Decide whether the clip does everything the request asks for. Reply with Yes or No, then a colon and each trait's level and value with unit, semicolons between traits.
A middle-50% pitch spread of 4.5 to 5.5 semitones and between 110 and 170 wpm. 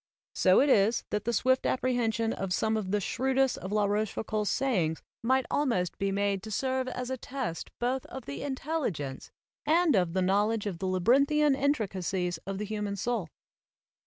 No: average, 5.1 semitones; average, 185 wpm